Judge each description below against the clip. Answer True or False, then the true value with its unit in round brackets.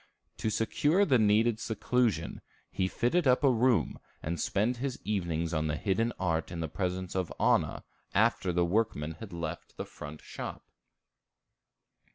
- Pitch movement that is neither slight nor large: False (5.7 semitones)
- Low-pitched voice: True (100 Hz)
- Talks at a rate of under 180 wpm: True (155 wpm)